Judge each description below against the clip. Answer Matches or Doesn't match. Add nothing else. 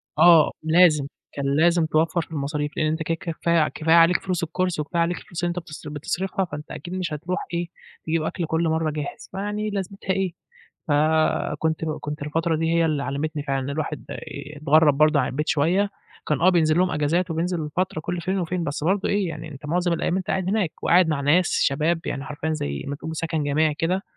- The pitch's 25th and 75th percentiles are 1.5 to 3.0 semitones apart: Matches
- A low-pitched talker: Doesn't match